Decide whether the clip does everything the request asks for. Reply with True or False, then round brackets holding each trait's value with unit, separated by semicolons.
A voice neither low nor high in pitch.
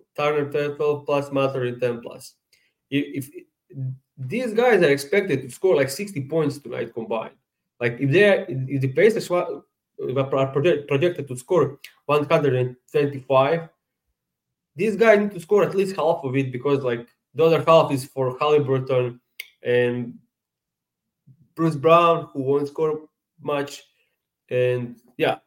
True (145 Hz)